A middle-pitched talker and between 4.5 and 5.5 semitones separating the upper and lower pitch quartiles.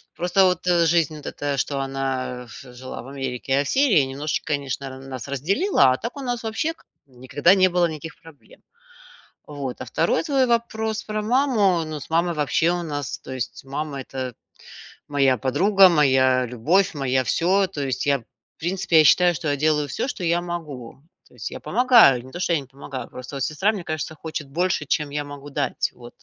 Yes: medium, 150 Hz; average, 5.0 semitones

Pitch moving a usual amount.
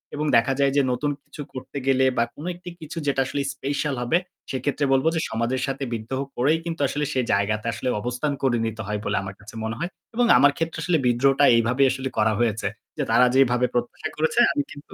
Yes: average, 3.4 semitones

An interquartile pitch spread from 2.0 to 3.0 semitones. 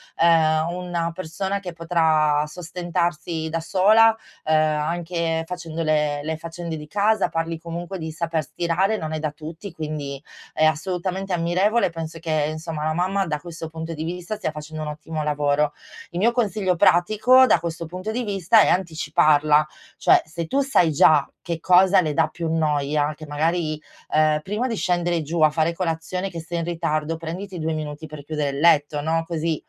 Yes: narrow, 2.4 semitones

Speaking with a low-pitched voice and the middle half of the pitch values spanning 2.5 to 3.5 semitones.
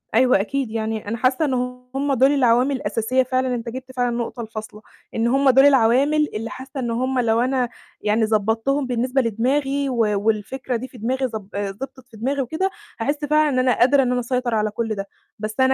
No: very high, 250 Hz; average, 3.0 semitones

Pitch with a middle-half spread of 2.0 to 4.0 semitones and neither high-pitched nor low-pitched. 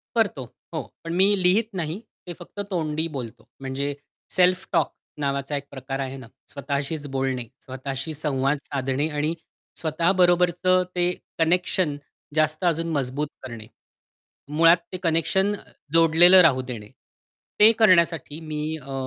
No: average, 4.4 semitones; medium, 155 Hz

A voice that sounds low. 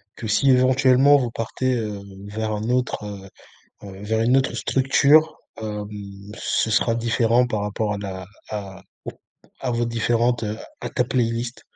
Yes: low, 115 Hz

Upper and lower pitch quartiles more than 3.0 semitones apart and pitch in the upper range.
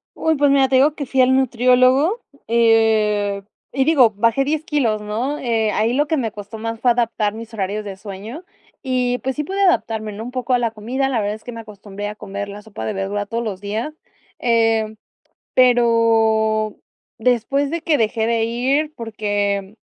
Yes: average, 3.5 semitones; high, 230 Hz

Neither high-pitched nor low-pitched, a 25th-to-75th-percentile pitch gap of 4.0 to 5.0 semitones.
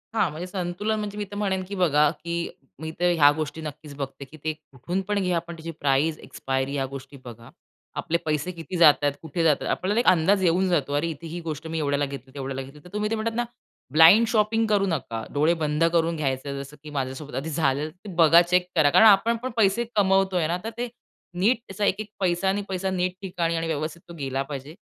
Yes: medium, 165 Hz; average, 4.7 semitones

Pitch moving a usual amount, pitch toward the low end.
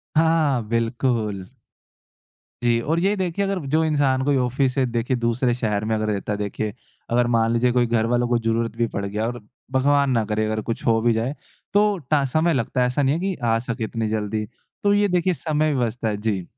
Yes: average, 4.2 semitones; low, 120 Hz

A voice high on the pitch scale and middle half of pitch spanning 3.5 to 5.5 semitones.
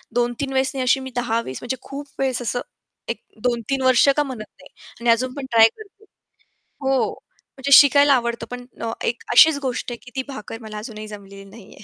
No: high, 245 Hz; average, 2.8 semitones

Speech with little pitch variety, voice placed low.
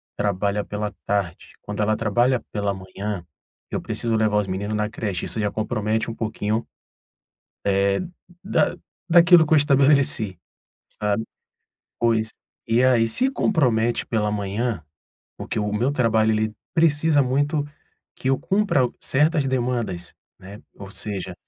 No: average, 4.2 semitones; low, 110 Hz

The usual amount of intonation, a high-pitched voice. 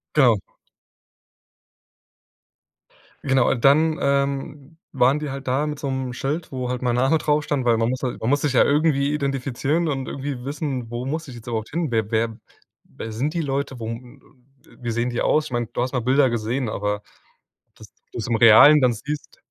No: average, 3.1 semitones; low, 130 Hz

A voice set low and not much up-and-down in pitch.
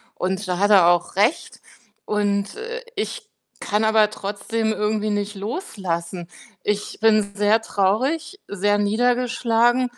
No: high, 210 Hz; narrow, 2.2 semitones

